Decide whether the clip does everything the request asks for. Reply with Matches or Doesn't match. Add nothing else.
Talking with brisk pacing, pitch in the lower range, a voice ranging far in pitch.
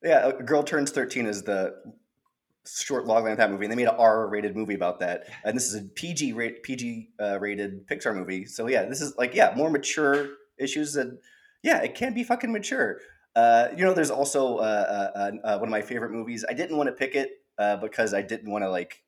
Matches